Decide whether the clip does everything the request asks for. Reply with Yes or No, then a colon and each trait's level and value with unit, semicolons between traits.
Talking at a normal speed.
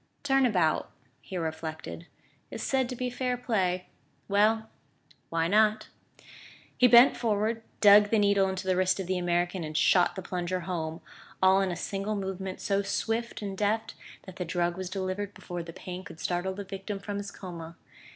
Yes: average, 180 wpm